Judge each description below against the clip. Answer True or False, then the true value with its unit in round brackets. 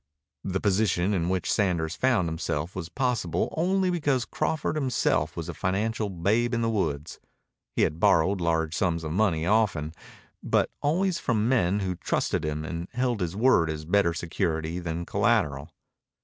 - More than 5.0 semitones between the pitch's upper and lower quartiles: True (5.5 semitones)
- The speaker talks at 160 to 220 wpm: True (165 wpm)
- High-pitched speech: False (95 Hz)